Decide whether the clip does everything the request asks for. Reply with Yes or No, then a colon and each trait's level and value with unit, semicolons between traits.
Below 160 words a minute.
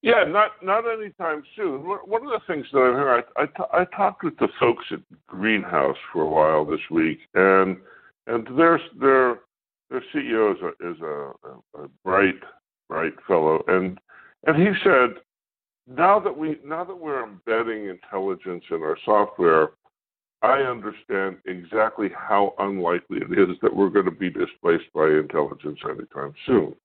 No: average, 165 wpm